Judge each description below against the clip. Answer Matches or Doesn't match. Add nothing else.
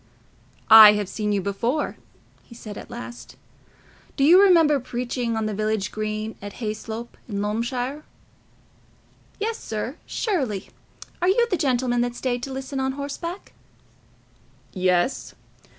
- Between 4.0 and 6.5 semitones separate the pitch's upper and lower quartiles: Matches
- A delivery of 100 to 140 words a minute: Matches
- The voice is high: Matches